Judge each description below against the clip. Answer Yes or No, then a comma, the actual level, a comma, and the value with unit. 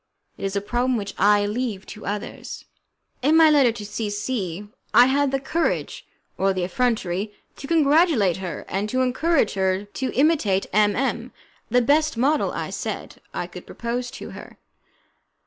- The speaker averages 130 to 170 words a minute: Yes, average, 165 wpm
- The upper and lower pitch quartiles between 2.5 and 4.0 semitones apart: No, average, 4.9 semitones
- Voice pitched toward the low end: No, high, 235 Hz